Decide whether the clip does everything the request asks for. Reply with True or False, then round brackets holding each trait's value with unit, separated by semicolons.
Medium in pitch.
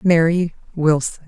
True (165 Hz)